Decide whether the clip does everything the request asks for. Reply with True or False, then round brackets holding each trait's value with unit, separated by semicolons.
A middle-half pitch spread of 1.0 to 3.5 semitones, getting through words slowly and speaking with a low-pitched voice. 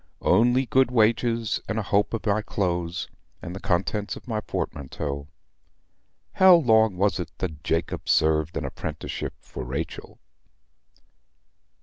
False (5.2 semitones; 130 wpm; 100 Hz)